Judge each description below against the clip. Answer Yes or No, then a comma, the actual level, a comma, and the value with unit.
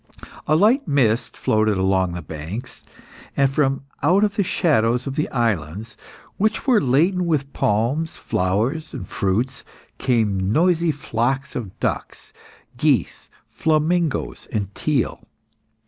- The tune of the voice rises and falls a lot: Yes, wide, 6.8 semitones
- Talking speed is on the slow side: Yes, slow, 120 wpm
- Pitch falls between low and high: No, low, 130 Hz